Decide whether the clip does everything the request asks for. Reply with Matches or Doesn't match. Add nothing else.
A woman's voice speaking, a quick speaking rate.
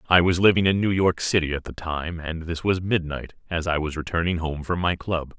Doesn't match